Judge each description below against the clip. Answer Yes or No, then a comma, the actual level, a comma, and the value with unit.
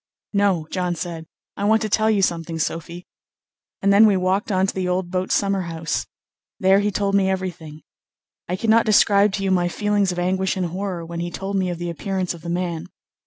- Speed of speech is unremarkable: No, fast, 215 wpm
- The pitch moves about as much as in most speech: No, narrow, 2.3 semitones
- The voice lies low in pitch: No, medium, 185 Hz